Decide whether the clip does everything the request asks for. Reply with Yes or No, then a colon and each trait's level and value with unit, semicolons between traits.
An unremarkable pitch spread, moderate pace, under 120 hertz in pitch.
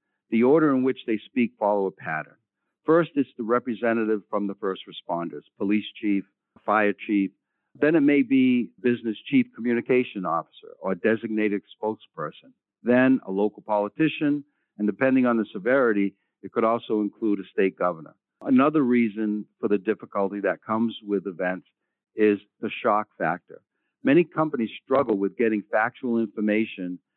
Yes: average, 3.4 semitones; average, 150 wpm; low, 110 Hz